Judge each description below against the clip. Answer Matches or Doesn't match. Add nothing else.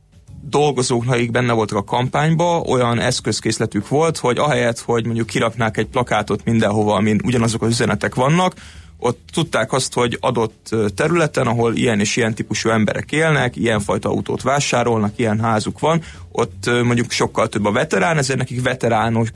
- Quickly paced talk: Matches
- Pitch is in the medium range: Doesn't match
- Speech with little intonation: Doesn't match